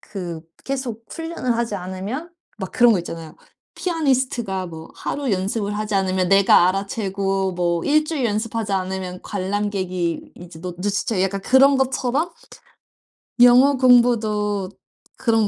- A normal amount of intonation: Yes, average, 4.8 semitones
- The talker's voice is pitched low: No, high, 205 Hz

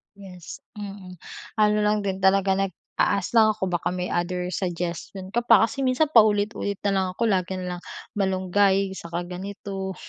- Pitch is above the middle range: Yes, high, 195 Hz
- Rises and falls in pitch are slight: Yes, narrow, 2.0 semitones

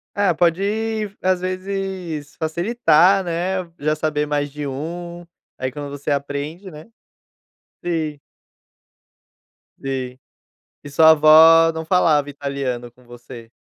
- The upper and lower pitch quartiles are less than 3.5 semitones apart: No, average, 4.1 semitones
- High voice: No, medium, 155 Hz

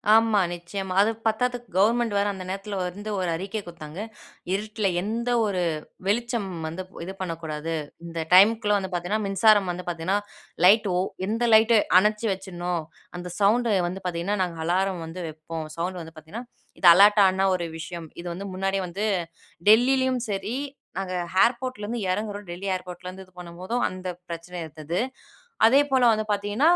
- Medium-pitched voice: No, high, 195 Hz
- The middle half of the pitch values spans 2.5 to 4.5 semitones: Yes, average, 3.6 semitones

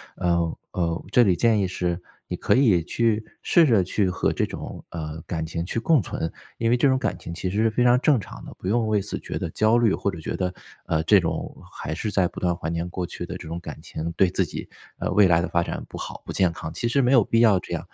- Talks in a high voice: No, very low, 95 Hz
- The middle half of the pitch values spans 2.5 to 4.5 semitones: No, average, 4.9 semitones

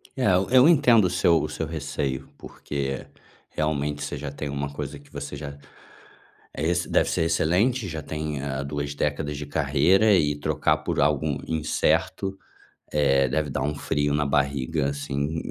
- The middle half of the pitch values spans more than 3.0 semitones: No, narrow, 2.5 semitones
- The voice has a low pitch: Yes, very low, 75 Hz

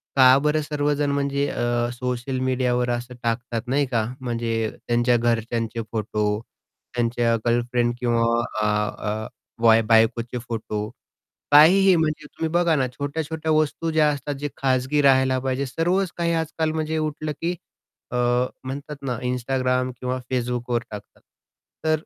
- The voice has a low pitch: Yes, low, 130 Hz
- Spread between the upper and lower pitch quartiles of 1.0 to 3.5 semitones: No, average, 3.9 semitones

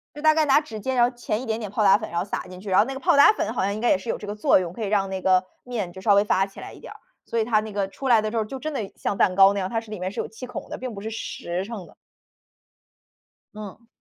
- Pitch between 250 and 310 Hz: No, high, 215 Hz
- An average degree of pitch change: Yes, average, 3.4 semitones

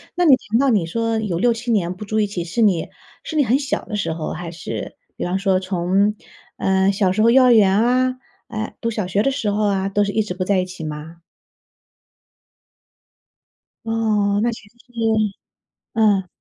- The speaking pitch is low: No, high, 205 Hz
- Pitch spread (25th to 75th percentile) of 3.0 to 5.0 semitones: Yes, average, 3.5 semitones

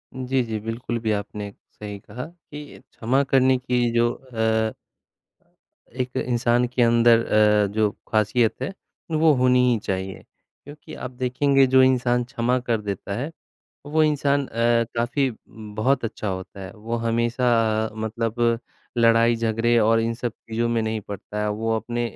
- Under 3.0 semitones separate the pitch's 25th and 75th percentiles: Yes, narrow, 2.4 semitones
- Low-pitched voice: Yes, low, 115 Hz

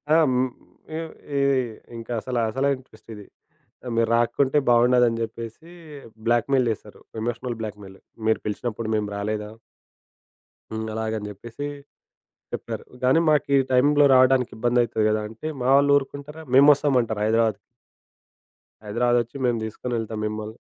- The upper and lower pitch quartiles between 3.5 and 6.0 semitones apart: No, average, 2.8 semitones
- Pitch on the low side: Yes, low, 120 Hz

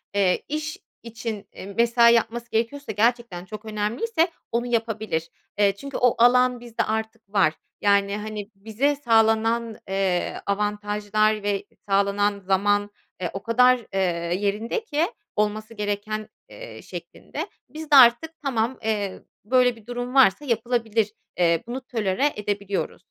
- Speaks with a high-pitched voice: Yes, high, 220 Hz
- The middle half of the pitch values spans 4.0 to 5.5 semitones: No, average, 2.8 semitones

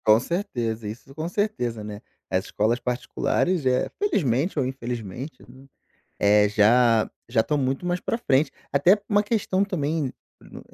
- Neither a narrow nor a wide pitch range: No, wide, 7.4 semitones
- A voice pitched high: No, low, 130 Hz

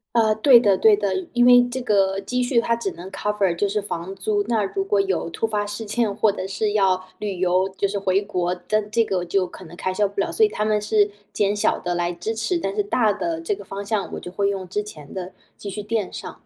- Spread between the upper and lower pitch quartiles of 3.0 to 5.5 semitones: No, narrow, 2.6 semitones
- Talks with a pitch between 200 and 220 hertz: Yes, high, 205 Hz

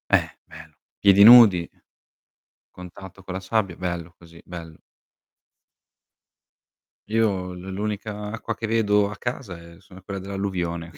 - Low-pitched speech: Yes, very low, 95 Hz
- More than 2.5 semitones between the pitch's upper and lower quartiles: Yes, average, 2.9 semitones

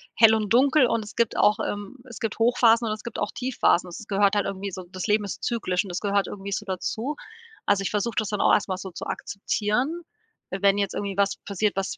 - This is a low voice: No, high, 205 Hz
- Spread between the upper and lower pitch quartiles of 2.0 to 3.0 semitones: Yes, narrow, 2.5 semitones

